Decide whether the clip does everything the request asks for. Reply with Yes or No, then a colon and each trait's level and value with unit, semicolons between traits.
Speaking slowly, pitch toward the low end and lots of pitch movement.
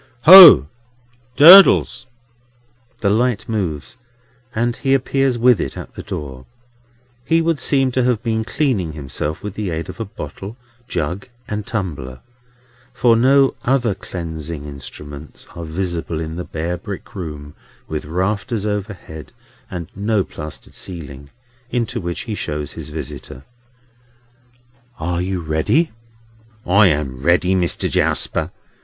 Yes: slow, 130 wpm; very low, 95 Hz; wide, 6.9 semitones